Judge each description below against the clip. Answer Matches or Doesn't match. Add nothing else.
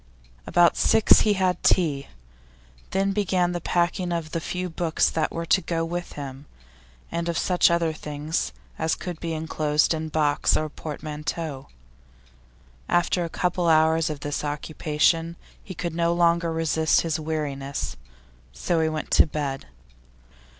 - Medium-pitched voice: Matches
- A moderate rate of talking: Matches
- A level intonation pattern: Matches